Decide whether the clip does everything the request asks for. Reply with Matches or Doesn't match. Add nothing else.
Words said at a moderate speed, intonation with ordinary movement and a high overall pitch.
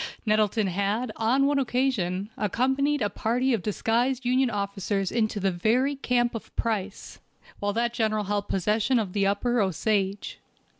Matches